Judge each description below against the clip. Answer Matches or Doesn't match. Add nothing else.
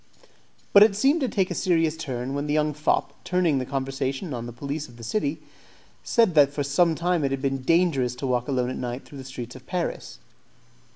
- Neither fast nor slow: Doesn't match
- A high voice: Doesn't match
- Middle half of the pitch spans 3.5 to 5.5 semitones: Matches